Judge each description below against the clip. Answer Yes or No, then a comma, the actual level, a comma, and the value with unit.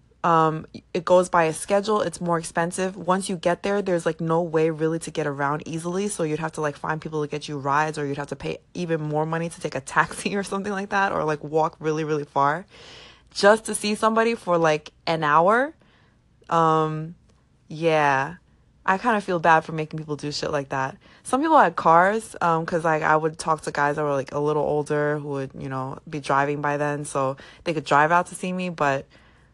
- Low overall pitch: No, medium, 160 Hz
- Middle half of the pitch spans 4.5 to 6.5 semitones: No, average, 3.2 semitones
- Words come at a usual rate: No, fast, 230 wpm